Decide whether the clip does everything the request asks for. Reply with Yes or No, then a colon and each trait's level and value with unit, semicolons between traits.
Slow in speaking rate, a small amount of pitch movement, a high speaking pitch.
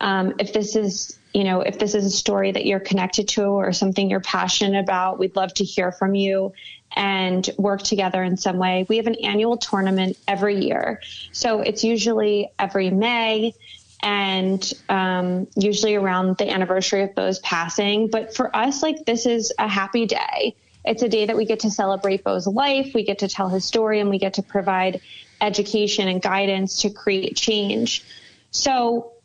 No: average, 185 wpm; narrow, 2.2 semitones; high, 200 Hz